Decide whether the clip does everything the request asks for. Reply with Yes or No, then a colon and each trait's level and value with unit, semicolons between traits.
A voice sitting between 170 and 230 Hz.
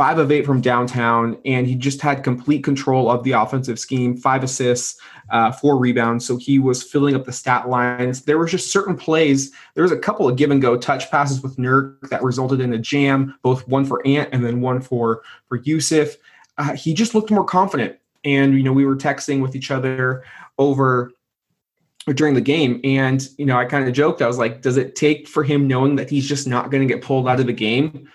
No: low, 135 Hz